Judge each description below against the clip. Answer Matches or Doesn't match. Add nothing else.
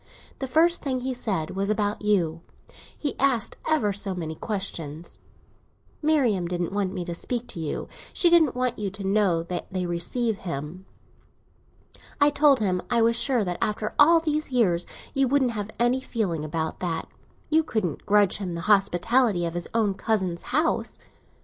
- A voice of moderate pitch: Doesn't match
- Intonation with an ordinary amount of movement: Doesn't match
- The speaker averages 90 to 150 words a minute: Doesn't match